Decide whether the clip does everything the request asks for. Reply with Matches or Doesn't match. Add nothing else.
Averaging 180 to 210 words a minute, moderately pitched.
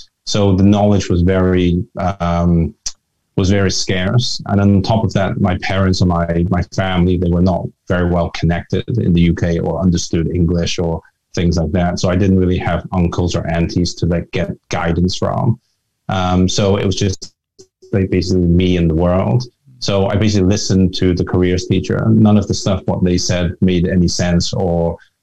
Doesn't match